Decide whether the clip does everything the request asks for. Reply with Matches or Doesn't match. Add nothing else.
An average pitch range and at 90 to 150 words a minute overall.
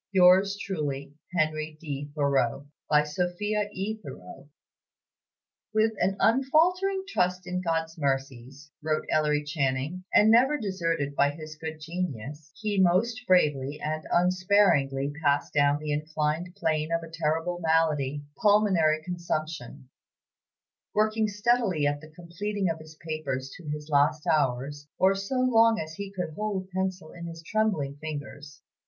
Matches